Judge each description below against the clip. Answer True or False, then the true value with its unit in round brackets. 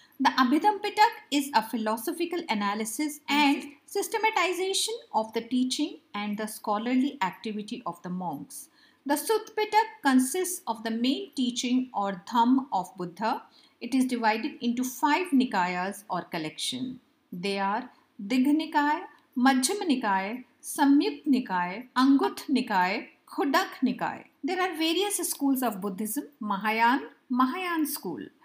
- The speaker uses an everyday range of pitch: False (5.7 semitones)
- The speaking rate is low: True (125 wpm)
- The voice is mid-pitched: False (255 Hz)